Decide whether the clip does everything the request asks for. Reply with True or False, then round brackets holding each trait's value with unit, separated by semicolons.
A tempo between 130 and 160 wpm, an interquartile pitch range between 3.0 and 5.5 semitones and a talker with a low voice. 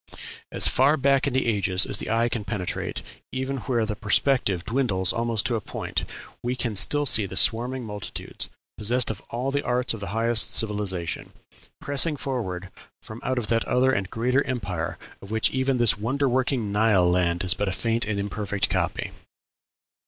False (175 wpm; 4.1 semitones; 115 Hz)